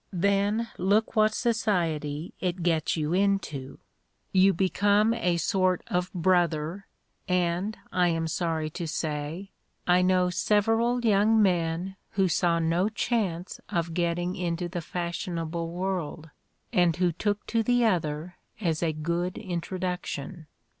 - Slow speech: Yes, slow, 130 wpm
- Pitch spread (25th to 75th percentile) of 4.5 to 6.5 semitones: No, average, 3.0 semitones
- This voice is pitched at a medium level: Yes, medium, 180 Hz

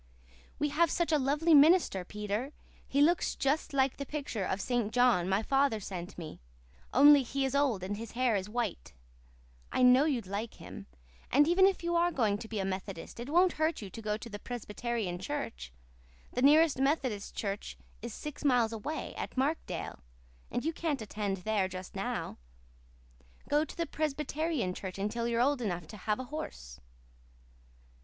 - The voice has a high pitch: Yes, high, 245 Hz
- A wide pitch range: Yes, wide, 6.1 semitones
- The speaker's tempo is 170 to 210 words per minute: Yes, average, 180 wpm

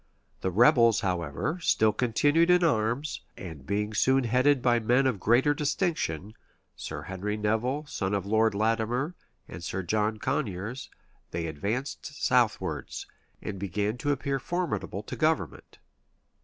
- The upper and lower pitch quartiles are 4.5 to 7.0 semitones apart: Yes, average, 5.1 semitones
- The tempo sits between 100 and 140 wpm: Yes, slow, 135 wpm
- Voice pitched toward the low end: Yes, low, 115 Hz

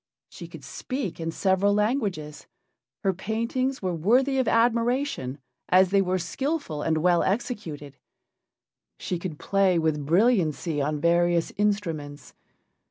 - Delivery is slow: Yes, slow, 125 wpm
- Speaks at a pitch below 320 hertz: Yes, medium, 185 Hz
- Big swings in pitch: Yes, wide, 6.1 semitones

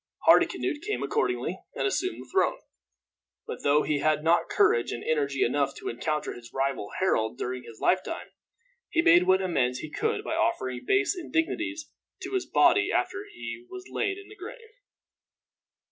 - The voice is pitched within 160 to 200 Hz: Yes, high, 190 Hz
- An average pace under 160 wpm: No, average, 165 wpm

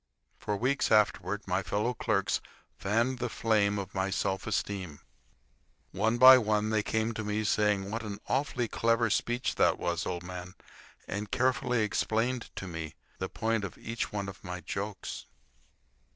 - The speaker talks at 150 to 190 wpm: Yes, average, 160 wpm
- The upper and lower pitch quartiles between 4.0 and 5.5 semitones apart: No, average, 3.0 semitones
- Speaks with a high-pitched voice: No, low, 105 Hz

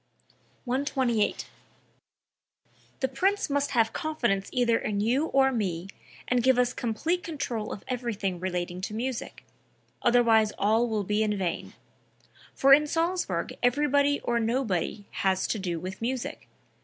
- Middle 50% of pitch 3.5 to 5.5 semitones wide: Yes, average, 4.5 semitones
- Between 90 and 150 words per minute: Yes, slow, 135 wpm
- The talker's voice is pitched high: Yes, high, 235 Hz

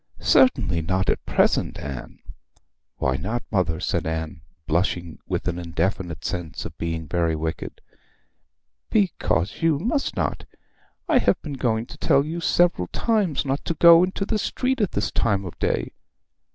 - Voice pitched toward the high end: No, low, 100 Hz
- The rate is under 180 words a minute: Yes, average, 155 wpm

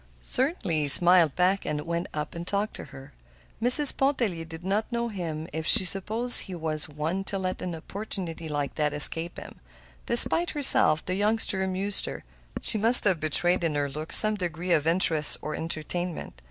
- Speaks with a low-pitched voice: No, medium, 175 Hz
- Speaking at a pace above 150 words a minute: Yes, average, 180 wpm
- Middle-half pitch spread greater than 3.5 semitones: Yes, average, 4.4 semitones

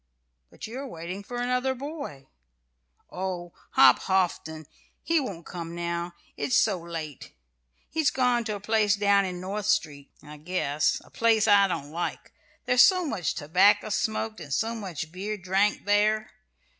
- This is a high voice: Yes, high, 195 Hz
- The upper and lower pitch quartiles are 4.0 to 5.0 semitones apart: Yes, average, 4.4 semitones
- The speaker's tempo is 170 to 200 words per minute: No, average, 155 wpm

